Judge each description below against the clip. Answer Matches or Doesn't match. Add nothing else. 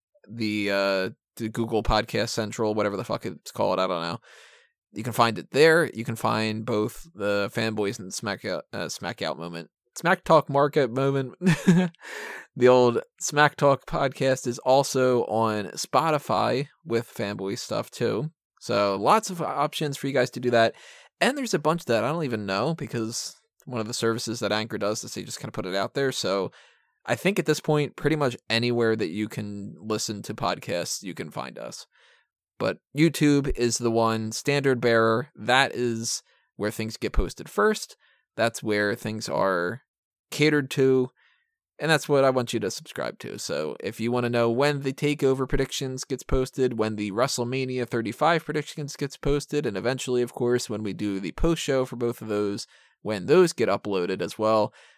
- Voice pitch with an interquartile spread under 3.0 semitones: Doesn't match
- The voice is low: Matches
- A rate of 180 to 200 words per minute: Matches